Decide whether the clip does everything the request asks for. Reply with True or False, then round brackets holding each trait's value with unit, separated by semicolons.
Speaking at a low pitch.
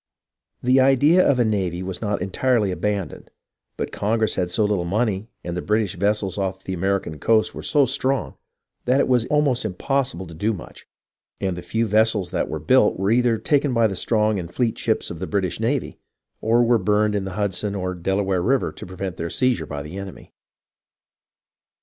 True (105 Hz)